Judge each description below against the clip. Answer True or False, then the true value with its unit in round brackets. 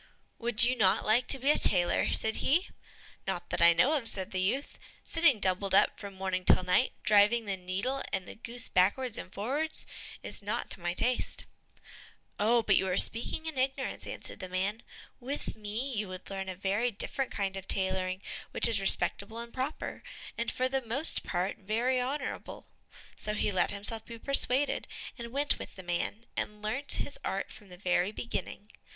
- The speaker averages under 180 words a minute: False (190 wpm)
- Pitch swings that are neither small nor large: True (4.9 semitones)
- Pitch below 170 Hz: False (215 Hz)